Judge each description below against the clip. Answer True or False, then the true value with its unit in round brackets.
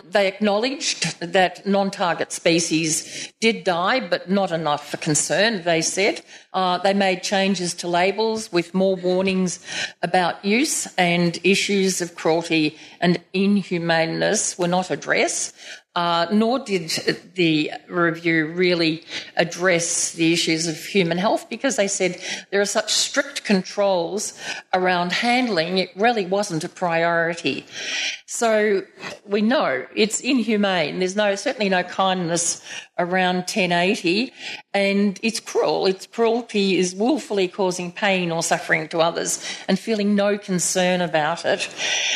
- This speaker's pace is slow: True (130 wpm)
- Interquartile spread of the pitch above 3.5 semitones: False (3.0 semitones)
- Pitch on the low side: False (185 Hz)